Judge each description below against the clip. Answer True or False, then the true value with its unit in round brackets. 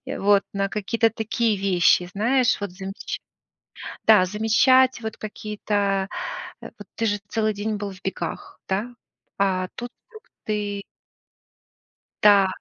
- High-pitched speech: True (205 Hz)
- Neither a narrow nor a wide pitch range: False (2.2 semitones)